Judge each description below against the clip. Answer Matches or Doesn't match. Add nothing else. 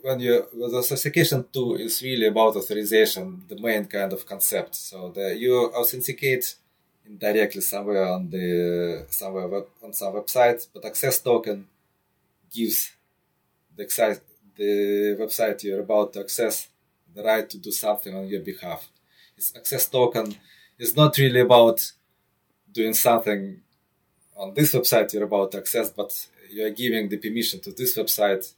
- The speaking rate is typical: Matches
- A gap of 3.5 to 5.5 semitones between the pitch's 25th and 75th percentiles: Matches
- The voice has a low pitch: Matches